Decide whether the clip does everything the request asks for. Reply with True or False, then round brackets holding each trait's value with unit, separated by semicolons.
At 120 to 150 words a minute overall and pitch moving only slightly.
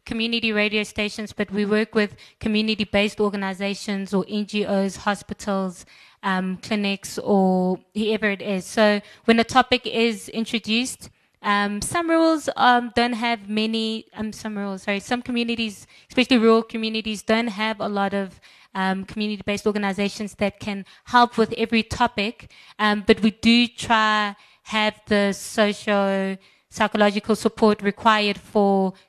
True (135 wpm; 1.9 semitones)